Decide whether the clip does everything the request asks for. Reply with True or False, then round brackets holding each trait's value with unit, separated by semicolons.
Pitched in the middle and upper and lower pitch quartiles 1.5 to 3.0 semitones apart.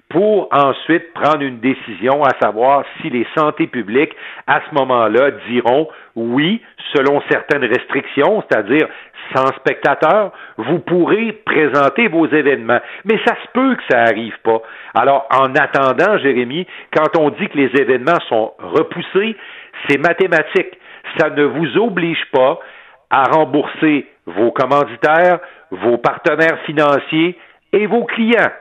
False (155 Hz; 4.6 semitones)